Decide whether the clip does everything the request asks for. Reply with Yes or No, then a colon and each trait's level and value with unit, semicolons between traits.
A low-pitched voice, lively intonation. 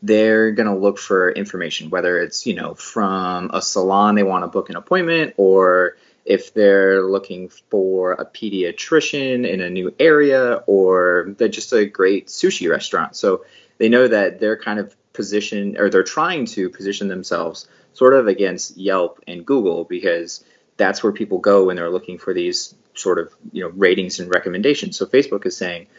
Yes: low, 100 Hz; wide, 8.4 semitones